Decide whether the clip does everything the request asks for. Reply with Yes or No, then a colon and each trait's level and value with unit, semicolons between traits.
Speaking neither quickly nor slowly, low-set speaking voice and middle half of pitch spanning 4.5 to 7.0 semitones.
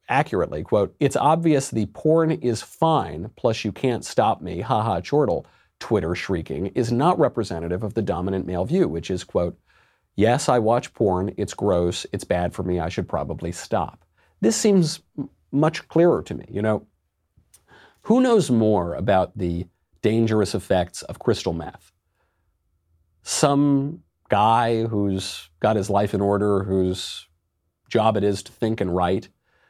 Yes: average, 160 wpm; low, 100 Hz; average, 5.2 semitones